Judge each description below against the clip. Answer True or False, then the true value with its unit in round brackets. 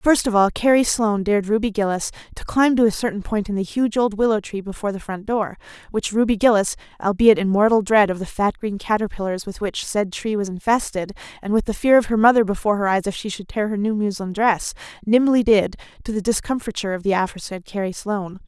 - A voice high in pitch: True (210 Hz)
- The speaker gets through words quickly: True (225 wpm)